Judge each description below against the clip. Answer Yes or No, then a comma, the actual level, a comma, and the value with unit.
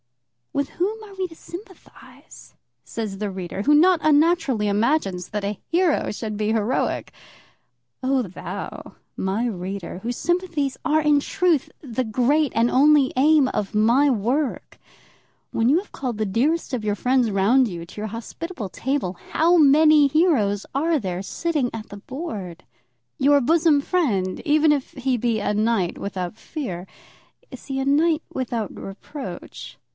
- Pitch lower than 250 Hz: No, very high, 260 Hz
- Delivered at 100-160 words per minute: Yes, average, 155 wpm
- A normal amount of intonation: No, wide, 6.5 semitones